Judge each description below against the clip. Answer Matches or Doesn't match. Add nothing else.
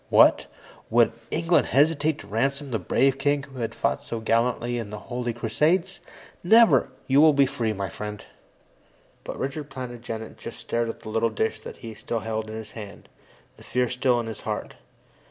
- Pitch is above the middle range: Doesn't match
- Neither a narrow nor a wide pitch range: Matches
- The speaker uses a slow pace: Doesn't match